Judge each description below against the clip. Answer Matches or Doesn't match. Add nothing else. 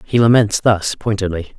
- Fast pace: Doesn't match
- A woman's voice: Doesn't match